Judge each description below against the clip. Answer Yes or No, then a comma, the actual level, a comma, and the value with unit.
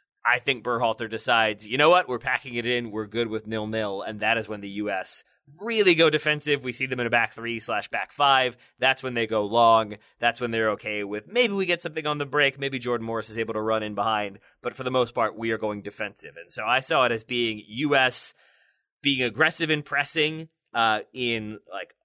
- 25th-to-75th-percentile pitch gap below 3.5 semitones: No, average, 4.2 semitones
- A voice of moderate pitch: No, low, 120 Hz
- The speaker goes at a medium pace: No, fast, 230 wpm